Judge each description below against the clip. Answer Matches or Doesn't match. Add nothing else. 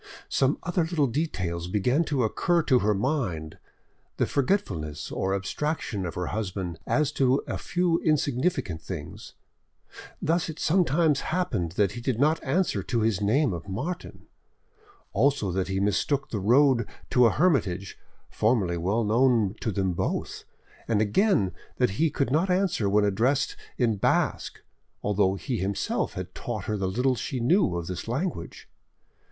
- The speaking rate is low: Doesn't match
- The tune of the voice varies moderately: Doesn't match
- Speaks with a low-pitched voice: Matches